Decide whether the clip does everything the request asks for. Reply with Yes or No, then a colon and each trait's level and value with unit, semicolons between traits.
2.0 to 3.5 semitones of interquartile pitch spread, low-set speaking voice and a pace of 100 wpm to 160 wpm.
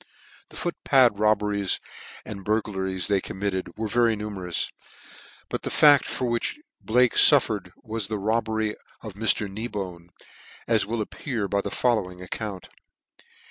Yes: average, 2.9 semitones; low, 105 Hz; average, 140 wpm